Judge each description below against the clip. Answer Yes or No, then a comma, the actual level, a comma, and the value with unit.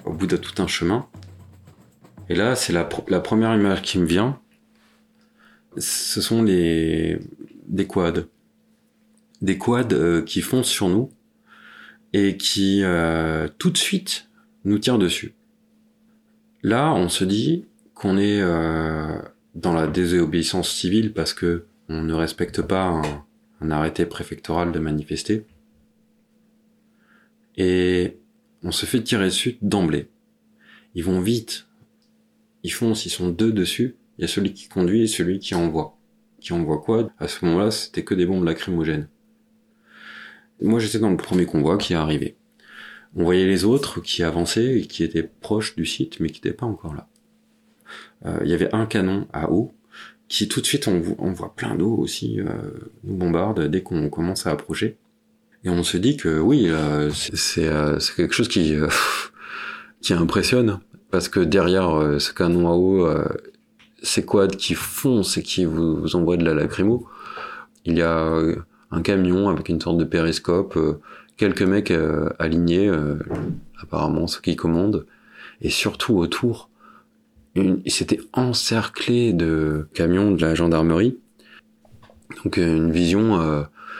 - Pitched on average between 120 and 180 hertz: No, very low, 95 Hz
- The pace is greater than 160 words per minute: No, average, 155 wpm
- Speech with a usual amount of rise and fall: No, wide, 6.9 semitones